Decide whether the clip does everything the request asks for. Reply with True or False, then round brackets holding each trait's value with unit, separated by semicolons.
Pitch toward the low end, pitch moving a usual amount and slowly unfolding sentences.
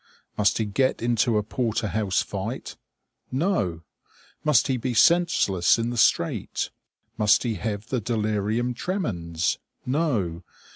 True (110 Hz; 3.8 semitones; 130 wpm)